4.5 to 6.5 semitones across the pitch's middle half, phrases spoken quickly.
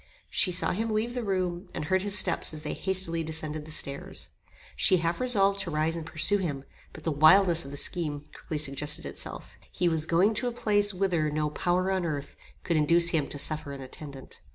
No: average, 3.9 semitones; fast, 210 wpm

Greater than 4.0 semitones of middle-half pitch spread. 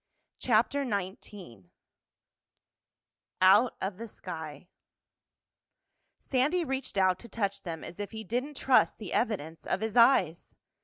Yes: average, 5.0 semitones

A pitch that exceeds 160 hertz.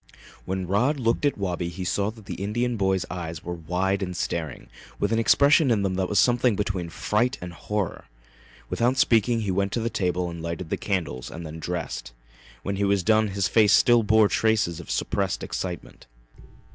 No: low, 100 Hz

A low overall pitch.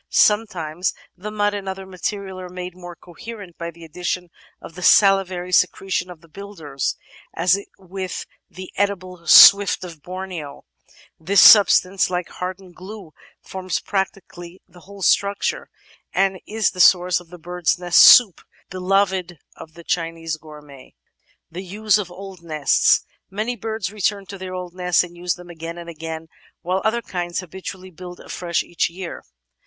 No: medium, 180 Hz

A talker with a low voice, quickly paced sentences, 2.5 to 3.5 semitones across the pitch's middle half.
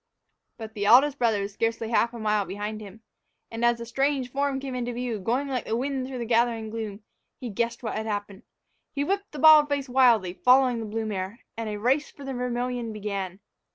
No: high, 235 Hz; fast, 215 wpm; average, 3.2 semitones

